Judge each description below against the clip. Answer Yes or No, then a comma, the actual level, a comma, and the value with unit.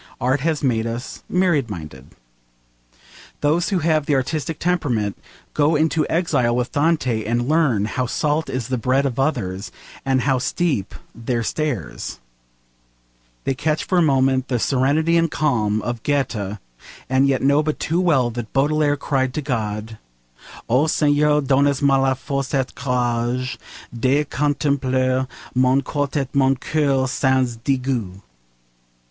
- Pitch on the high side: No, low, 135 Hz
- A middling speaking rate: Yes, average, 145 wpm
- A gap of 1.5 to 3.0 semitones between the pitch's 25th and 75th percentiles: No, average, 3.4 semitones